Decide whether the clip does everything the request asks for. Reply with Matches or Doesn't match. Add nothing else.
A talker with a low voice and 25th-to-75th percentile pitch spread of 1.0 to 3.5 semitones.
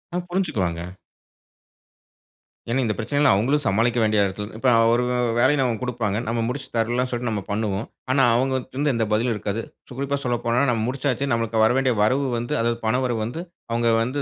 Matches